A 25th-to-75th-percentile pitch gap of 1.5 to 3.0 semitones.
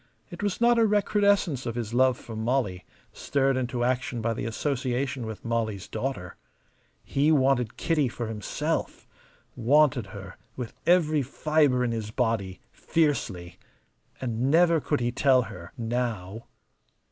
No: average, 4.3 semitones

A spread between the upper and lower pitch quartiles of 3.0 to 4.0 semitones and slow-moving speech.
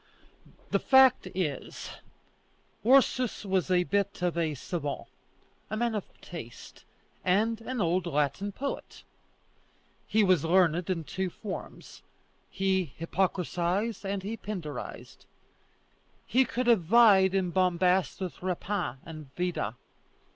Yes: average, 3.5 semitones; slow, 120 wpm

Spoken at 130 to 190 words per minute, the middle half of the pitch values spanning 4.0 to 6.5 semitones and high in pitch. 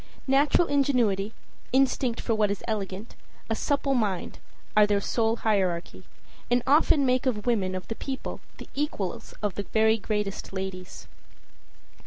Yes: average, 145 wpm; average, 4.6 semitones; high, 220 Hz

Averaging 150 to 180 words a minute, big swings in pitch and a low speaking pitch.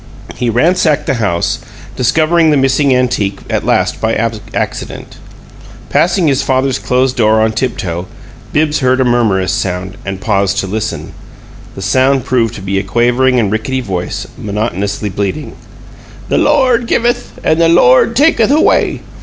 Yes: average, 155 wpm; wide, 6.2 semitones; low, 125 Hz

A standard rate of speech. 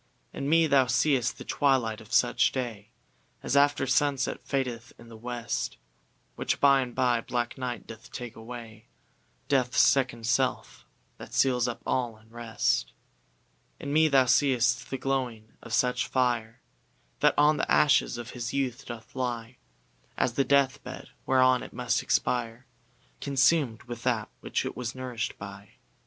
Yes: average, 155 wpm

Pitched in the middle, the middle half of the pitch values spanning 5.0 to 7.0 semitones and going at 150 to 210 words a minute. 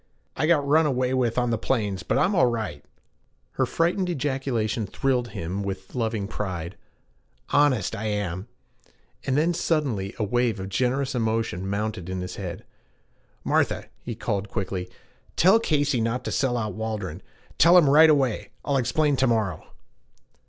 No: low, 115 Hz; wide, 5.5 semitones; average, 160 wpm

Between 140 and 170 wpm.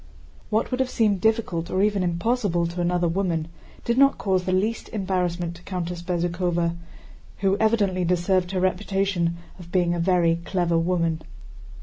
Yes: average, 155 wpm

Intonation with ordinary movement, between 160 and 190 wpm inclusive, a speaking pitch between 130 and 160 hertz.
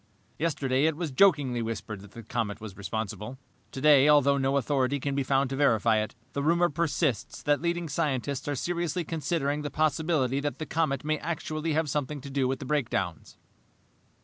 Yes: average, 3.3 semitones; average, 180 wpm; medium, 140 Hz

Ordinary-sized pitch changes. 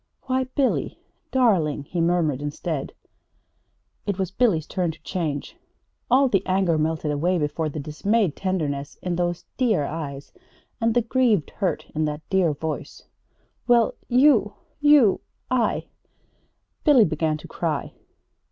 No: wide, 6.8 semitones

